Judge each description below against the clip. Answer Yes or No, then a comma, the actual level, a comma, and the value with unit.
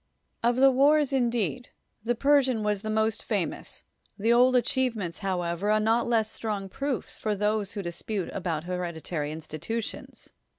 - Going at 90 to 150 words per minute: Yes, average, 145 wpm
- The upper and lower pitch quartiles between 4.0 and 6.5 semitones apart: Yes, average, 4.4 semitones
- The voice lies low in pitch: No, high, 215 Hz